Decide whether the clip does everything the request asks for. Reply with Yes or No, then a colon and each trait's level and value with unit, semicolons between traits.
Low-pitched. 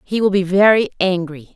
No: medium, 185 Hz